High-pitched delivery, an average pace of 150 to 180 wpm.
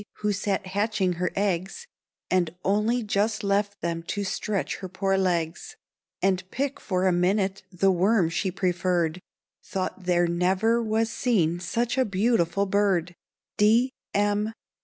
No: high, 195 Hz; average, 140 wpm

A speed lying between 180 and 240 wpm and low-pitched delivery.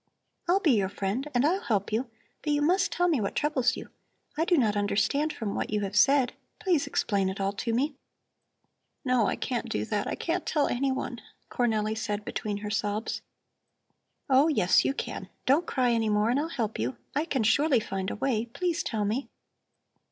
No: average, 195 wpm; high, 240 Hz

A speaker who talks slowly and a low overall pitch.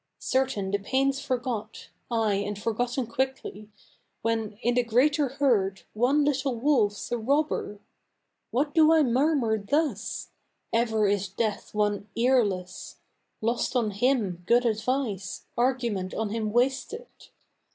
No: slow, 125 wpm; high, 235 Hz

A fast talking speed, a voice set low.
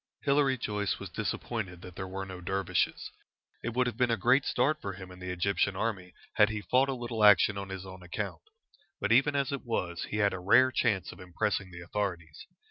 Yes: fast, 215 wpm; low, 100 Hz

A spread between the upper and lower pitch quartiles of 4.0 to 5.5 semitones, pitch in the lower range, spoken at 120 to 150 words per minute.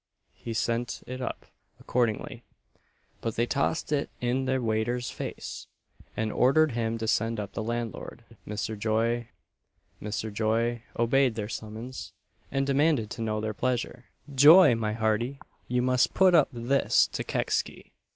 No: narrow, 2.6 semitones; low, 120 Hz; average, 145 wpm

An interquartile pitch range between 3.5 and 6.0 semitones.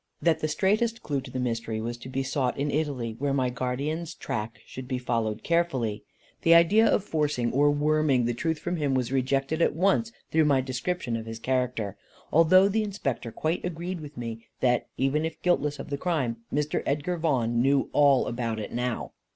Yes: average, 4.6 semitones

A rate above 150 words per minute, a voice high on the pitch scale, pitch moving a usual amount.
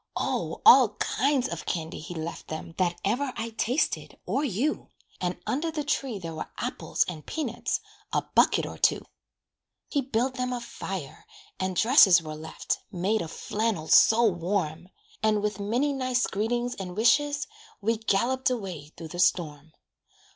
No: average, 160 wpm; high, 210 Hz; wide, 6.4 semitones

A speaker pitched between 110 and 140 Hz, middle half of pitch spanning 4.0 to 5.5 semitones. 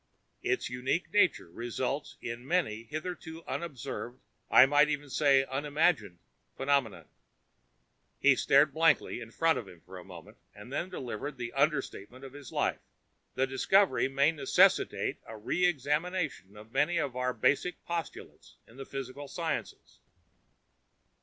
Yes: low, 135 Hz; average, 4.9 semitones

